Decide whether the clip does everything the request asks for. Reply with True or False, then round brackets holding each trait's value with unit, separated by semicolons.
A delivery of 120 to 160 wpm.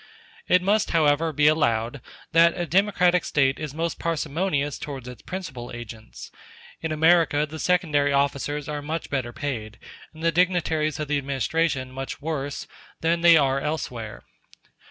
True (150 wpm)